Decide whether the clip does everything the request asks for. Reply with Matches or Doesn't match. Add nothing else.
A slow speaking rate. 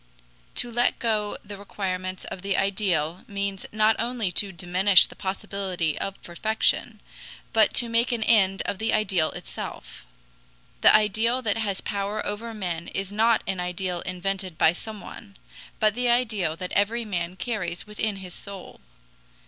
Doesn't match